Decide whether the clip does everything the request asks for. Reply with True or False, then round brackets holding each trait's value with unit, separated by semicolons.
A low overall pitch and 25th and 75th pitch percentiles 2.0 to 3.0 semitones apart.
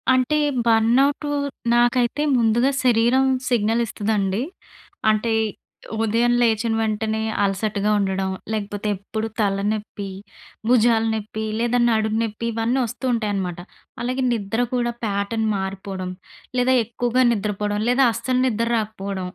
False (220 Hz; 2.6 semitones)